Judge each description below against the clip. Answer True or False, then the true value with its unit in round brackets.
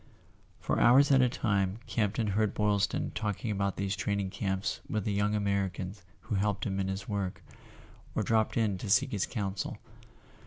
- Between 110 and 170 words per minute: False (185 wpm)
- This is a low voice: True (100 Hz)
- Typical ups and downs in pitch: False (1.8 semitones)